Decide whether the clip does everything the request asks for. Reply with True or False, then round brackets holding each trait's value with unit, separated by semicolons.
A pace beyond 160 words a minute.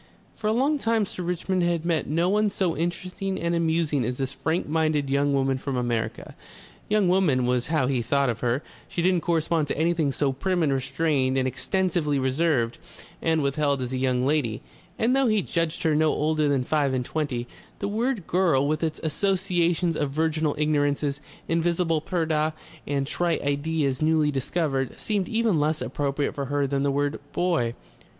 True (185 wpm)